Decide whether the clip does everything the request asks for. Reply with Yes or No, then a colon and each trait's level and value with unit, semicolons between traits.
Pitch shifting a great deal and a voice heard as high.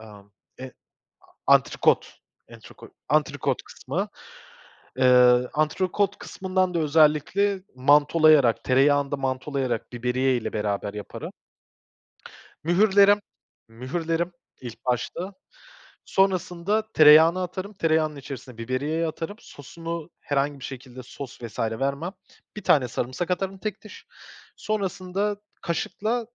No: wide, 6.3 semitones; medium, 150 Hz